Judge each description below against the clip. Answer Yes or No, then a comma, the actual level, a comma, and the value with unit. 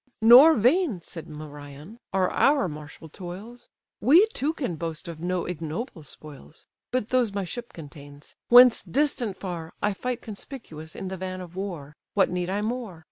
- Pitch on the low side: No, medium, 185 Hz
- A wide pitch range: Yes, wide, 6.9 semitones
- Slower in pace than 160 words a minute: No, average, 165 wpm